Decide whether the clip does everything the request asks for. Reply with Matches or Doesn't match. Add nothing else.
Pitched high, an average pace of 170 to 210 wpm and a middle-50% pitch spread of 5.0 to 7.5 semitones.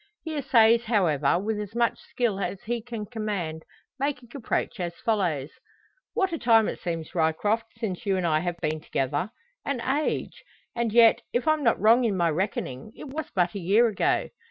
Matches